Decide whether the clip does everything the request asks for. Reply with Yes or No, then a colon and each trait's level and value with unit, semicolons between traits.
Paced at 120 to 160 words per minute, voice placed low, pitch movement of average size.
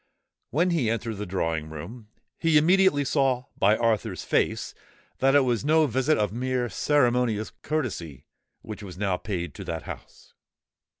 No: average, 155 wpm; low, 120 Hz; wide, 6.1 semitones